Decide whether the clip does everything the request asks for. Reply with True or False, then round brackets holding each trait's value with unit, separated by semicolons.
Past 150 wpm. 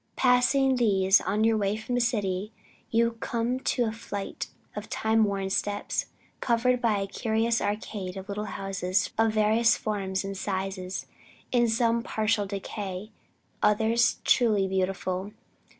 False (140 wpm)